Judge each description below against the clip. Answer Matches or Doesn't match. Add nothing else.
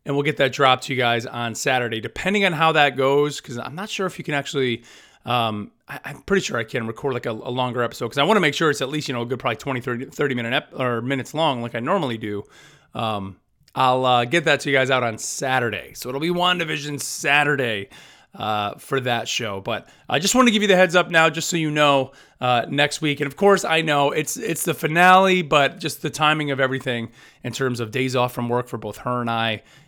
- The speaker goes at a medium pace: Doesn't match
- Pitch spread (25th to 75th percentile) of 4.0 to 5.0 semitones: Matches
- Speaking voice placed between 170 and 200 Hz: Doesn't match